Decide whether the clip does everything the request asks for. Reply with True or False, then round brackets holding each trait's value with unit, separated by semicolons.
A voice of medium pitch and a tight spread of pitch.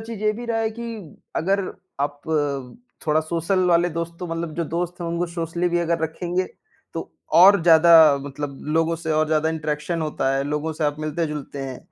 True (165 Hz; 2.3 semitones)